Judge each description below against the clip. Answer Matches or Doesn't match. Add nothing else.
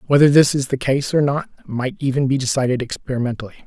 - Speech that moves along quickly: Doesn't match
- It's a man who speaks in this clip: Matches